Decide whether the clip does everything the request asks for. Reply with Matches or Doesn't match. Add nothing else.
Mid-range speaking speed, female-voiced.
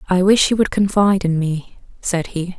Doesn't match